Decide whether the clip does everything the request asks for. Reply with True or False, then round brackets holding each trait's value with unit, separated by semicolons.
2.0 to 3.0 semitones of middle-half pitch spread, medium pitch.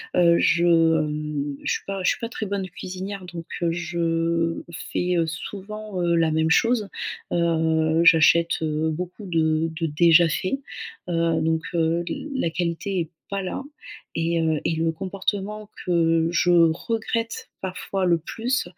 True (2.5 semitones; 170 Hz)